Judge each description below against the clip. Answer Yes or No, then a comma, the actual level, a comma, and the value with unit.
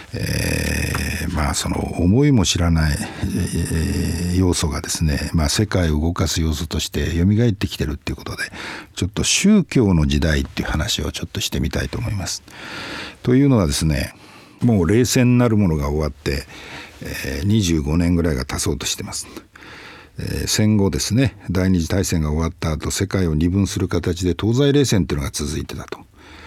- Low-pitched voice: Yes, very low, 90 Hz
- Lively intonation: No, average, 4.2 semitones